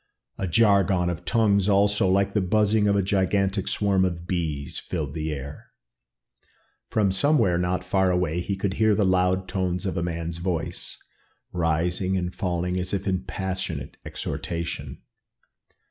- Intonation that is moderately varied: No, narrow, 2.3 semitones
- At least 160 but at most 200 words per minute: No, average, 150 wpm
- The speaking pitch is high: No, very low, 95 Hz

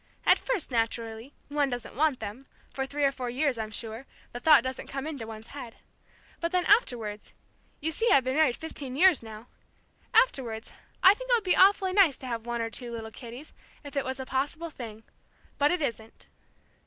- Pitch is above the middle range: Yes, very high, 265 Hz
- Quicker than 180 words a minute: Yes, average, 200 wpm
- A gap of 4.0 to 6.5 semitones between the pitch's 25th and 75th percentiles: Yes, average, 5.1 semitones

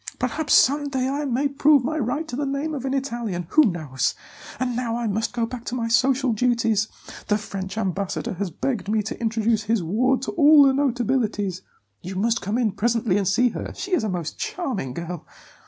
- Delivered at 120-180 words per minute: No, fast, 205 wpm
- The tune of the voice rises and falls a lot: No, average, 4.7 semitones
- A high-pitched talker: Yes, high, 235 Hz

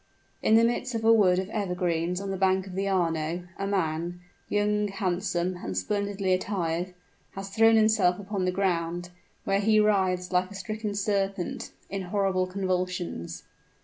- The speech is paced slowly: No, average, 160 wpm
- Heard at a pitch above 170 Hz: Yes, high, 190 Hz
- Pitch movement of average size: No, narrow, 2.2 semitones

